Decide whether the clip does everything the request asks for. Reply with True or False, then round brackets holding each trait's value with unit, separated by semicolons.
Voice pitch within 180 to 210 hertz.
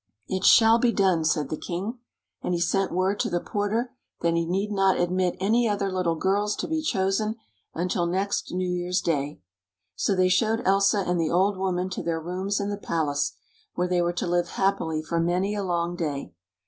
True (185 Hz)